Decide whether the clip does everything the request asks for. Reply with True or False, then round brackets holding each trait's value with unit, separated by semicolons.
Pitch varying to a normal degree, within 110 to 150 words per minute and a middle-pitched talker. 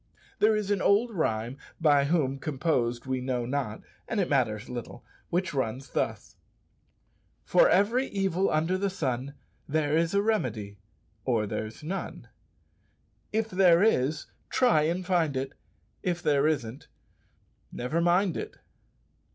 False (6.5 semitones; 135 wpm; 155 Hz)